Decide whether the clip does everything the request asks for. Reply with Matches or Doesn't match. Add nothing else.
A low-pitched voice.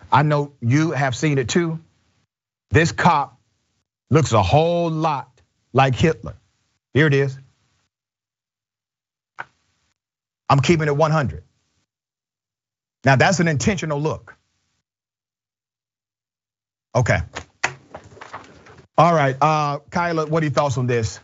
Matches